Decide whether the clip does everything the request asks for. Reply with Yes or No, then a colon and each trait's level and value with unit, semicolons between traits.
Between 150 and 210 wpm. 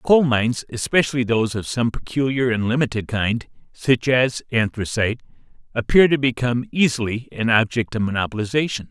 No: average, 140 wpm